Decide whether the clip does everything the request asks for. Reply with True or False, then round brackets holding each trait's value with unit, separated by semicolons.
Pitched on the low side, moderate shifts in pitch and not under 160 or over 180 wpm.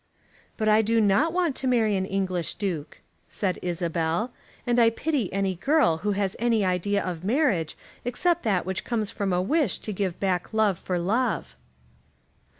False (200 Hz; 4.4 semitones; 170 wpm)